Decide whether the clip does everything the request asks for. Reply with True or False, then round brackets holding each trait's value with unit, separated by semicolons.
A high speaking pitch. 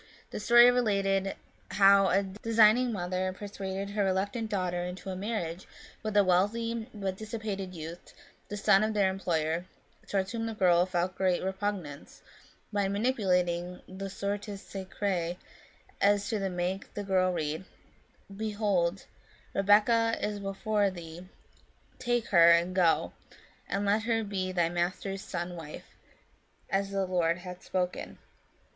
True (195 Hz)